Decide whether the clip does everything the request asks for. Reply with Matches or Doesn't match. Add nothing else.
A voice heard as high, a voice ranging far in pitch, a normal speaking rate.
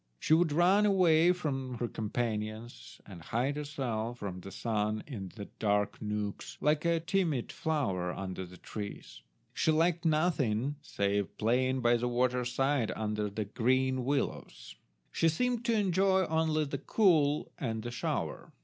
Doesn't match